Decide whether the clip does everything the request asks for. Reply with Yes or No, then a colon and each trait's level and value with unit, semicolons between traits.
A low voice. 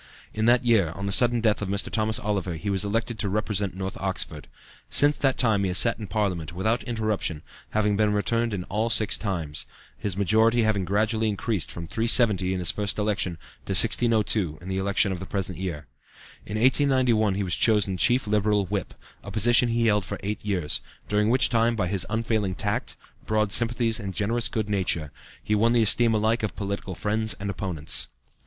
Yes: low, 105 Hz